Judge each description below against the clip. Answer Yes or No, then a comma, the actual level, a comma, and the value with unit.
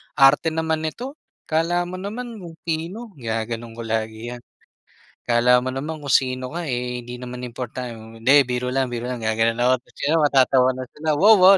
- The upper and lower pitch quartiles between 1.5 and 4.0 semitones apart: No, average, 5.0 semitones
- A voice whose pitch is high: No, low, 130 Hz